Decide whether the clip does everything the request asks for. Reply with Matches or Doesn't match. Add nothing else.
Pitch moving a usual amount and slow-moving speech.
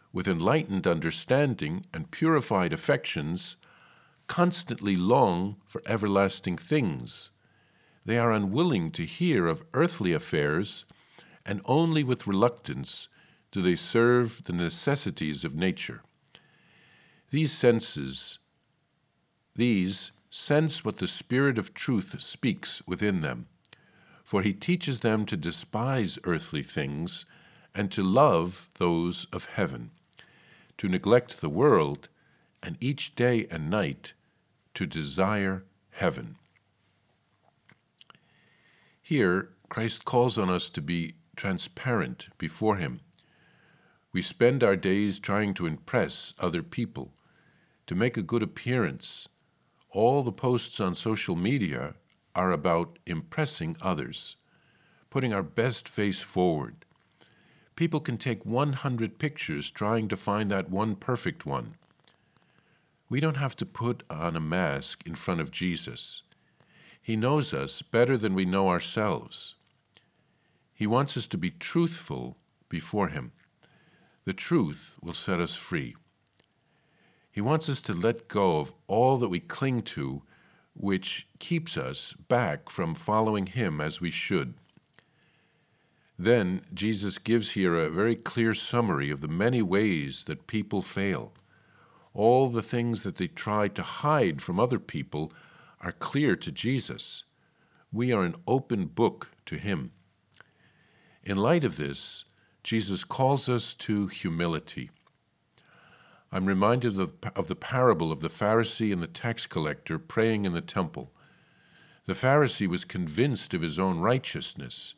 Doesn't match